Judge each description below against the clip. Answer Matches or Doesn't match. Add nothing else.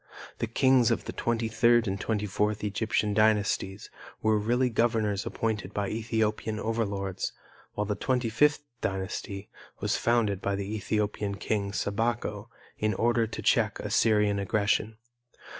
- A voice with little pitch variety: Matches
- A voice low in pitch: Matches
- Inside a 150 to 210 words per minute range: Doesn't match